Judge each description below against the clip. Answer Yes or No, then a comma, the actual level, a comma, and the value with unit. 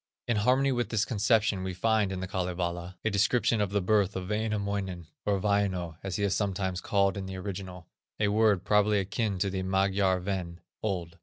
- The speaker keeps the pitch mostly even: Yes, narrow, 2.2 semitones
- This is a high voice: No, low, 100 Hz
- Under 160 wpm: No, average, 190 wpm